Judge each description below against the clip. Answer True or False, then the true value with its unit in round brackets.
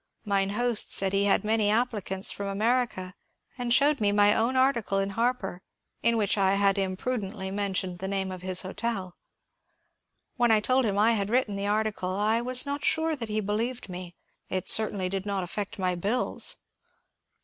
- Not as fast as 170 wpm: False (185 wpm)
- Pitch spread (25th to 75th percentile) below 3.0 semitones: False (3.3 semitones)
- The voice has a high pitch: True (205 Hz)